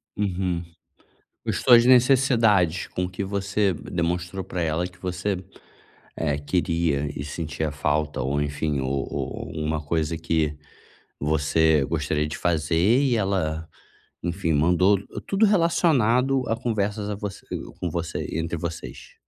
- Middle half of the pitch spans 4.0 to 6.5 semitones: Yes, average, 4.7 semitones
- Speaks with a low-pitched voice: Yes, very low, 85 Hz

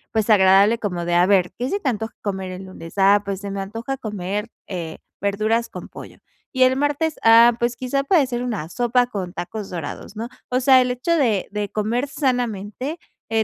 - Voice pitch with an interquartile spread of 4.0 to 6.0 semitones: Yes, average, 4.3 semitones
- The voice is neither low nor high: No, high, 220 Hz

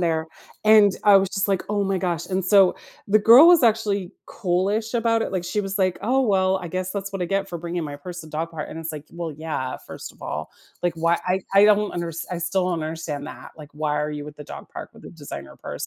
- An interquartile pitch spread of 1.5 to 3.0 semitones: No, average, 3.6 semitones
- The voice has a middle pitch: Yes, medium, 180 Hz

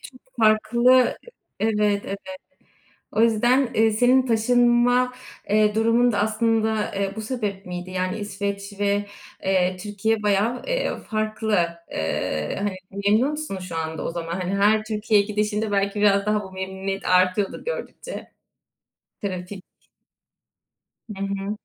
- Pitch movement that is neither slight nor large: No, narrow, 2.2 semitones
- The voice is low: No, high, 210 Hz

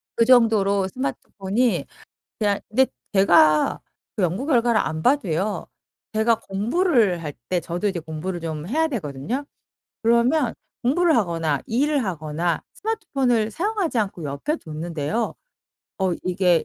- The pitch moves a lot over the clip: Yes, wide, 6.6 semitones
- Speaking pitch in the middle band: No, high, 205 Hz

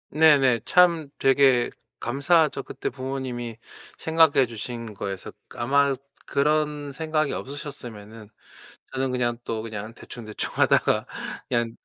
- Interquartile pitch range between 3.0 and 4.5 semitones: Yes, average, 3.8 semitones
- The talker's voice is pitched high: No, low, 130 Hz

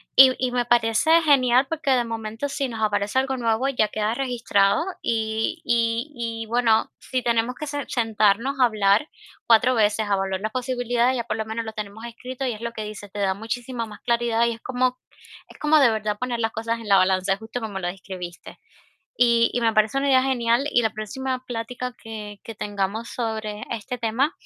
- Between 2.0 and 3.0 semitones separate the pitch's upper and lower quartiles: Yes, average, 2.7 semitones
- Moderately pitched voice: No, high, 230 Hz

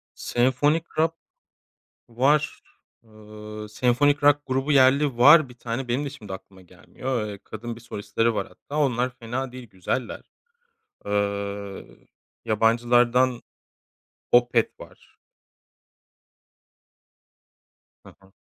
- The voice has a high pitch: No, low, 120 Hz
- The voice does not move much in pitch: No, average, 3.8 semitones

